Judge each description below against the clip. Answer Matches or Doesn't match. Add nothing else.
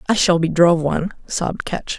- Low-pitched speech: Doesn't match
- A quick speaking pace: Matches